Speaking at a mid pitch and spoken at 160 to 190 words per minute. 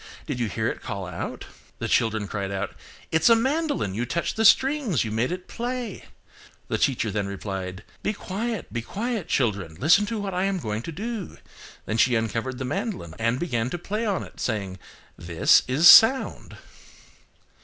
No: low, 130 Hz; average, 175 wpm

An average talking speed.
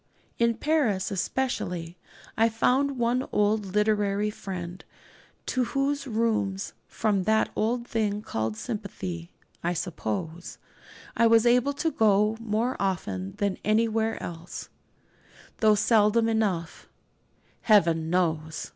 No: slow, 110 wpm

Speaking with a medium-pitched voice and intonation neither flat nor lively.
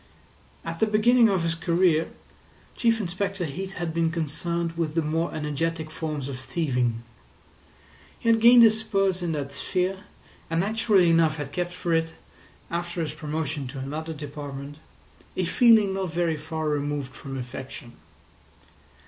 Yes: medium, 165 Hz; average, 3.7 semitones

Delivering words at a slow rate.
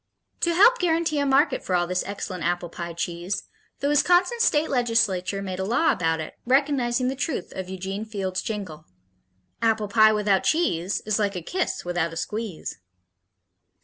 No: average, 170 wpm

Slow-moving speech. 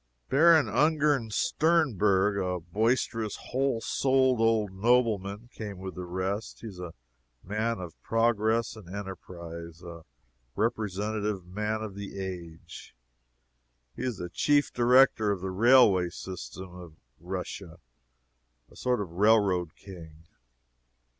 Yes: slow, 120 wpm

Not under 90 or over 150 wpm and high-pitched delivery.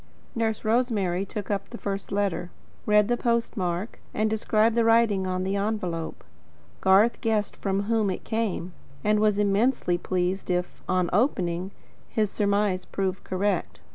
Yes: average, 145 wpm; high, 200 Hz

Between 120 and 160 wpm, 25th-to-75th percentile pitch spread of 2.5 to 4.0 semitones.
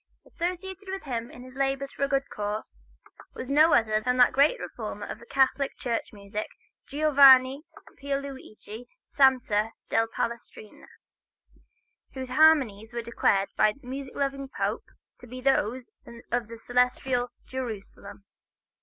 Yes: average, 140 wpm; average, 3.4 semitones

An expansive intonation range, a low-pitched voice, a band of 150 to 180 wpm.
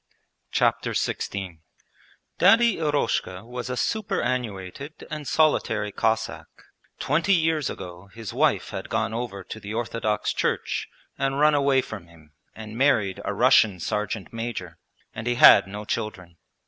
No: wide, 6.0 semitones; low, 115 Hz; slow, 135 wpm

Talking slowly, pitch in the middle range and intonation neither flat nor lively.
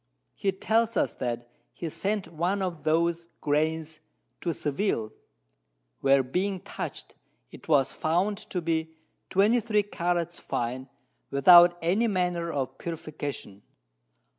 Yes: slow, 115 wpm; medium, 170 Hz; average, 4.2 semitones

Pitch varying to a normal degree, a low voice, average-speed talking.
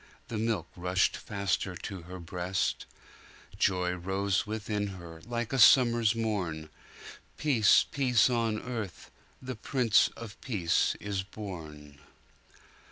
No: average, 4.1 semitones; low, 100 Hz; slow, 105 wpm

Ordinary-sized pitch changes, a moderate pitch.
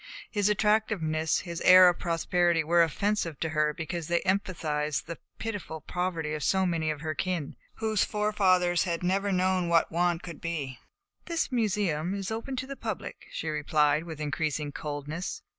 Yes: average, 3.8 semitones; medium, 170 Hz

